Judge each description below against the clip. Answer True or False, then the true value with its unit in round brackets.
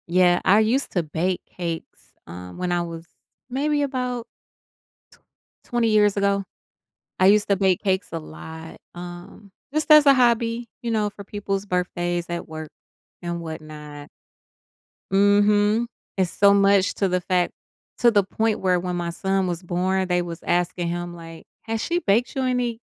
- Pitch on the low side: False (190 Hz)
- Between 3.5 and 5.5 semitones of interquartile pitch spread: True (3.8 semitones)